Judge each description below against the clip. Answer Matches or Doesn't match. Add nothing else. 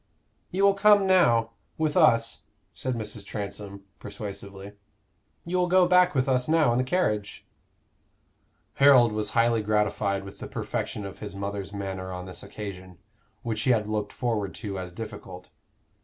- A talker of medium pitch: Doesn't match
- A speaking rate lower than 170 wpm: Matches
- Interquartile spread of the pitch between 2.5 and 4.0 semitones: Doesn't match